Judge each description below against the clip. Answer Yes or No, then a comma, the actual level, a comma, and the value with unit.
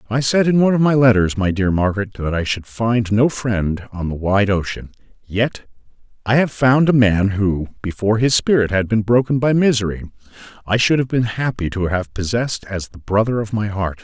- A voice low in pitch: Yes, low, 110 Hz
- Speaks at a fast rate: Yes, fast, 210 wpm